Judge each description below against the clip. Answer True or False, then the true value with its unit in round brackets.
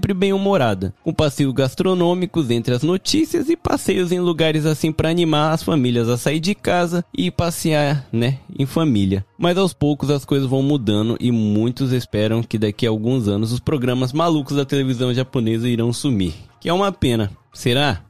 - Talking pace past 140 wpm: True (180 wpm)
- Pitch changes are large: True (5.9 semitones)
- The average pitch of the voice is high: False (140 Hz)